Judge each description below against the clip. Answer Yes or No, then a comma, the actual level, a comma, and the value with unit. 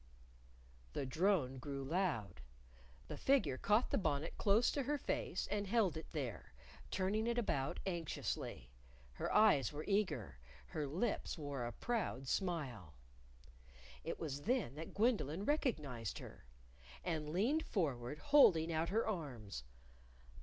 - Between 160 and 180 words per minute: No, slow, 135 wpm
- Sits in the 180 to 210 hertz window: No, medium, 160 Hz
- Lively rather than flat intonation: Yes, wide, 7.7 semitones